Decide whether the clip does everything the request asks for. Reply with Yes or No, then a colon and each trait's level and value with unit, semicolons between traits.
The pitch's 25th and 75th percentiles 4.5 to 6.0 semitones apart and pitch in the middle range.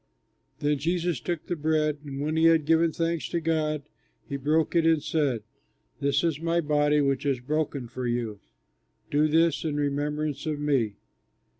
No: narrow, 2.4 semitones; medium, 150 Hz